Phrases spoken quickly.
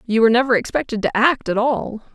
Yes: fast, 225 wpm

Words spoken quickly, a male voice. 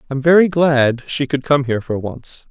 Yes: fast, 215 wpm; male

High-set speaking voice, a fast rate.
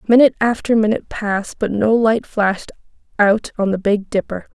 No: high, 215 Hz; average, 170 wpm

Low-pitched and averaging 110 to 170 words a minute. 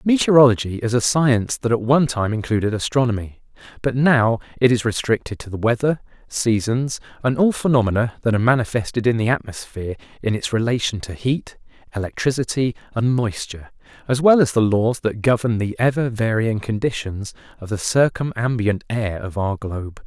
Yes: low, 115 Hz; average, 160 wpm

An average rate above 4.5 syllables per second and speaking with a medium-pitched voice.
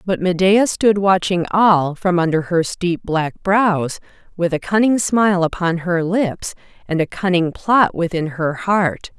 No: 4.0 syllables/s; medium, 180 Hz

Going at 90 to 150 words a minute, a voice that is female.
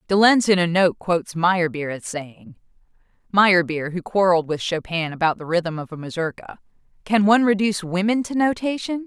No: average, 160 wpm; female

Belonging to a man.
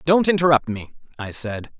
Yes: male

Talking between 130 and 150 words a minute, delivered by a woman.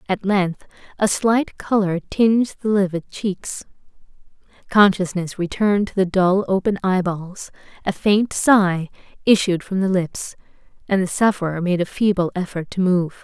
Yes: average, 145 wpm; female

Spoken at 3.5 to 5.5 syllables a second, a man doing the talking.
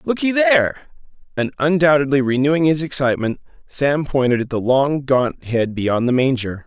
Yes: 5.0 syllables/s; male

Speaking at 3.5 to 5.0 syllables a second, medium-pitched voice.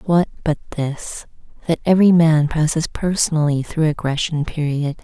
Yes: 4.9 syllables/s; medium, 155 Hz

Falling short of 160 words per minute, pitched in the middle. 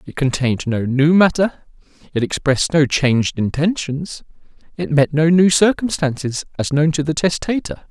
Yes: average, 150 wpm; medium, 150 Hz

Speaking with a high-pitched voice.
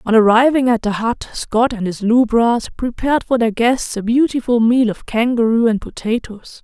Yes: high, 235 Hz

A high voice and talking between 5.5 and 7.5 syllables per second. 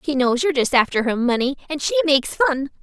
Yes: very high, 280 Hz; 6.4 syllables/s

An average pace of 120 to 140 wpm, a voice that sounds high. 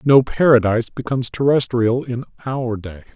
No: slow, 135 wpm; low, 120 Hz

